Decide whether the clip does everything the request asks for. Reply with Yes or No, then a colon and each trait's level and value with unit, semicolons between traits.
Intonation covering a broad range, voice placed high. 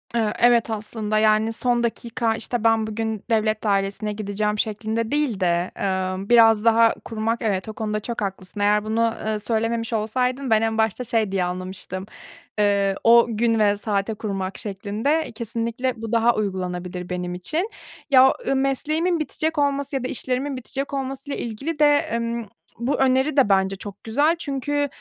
No: average, 3.5 semitones; high, 225 Hz